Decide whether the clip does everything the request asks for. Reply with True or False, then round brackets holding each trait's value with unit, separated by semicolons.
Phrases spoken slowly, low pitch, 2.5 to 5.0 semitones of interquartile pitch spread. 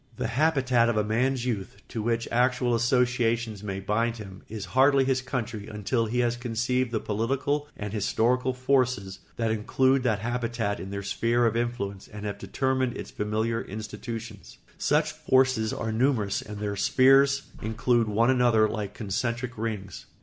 False (160 wpm; 115 Hz; 3.0 semitones)